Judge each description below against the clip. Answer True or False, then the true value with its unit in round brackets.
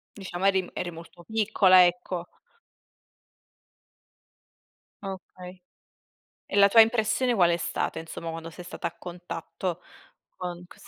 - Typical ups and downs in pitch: False (2.3 semitones)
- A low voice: False (180 Hz)